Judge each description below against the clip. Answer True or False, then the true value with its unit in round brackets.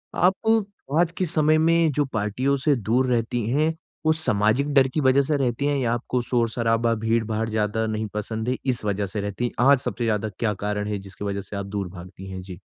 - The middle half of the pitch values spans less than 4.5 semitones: False (4.9 semitones)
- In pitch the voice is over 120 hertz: False (115 Hz)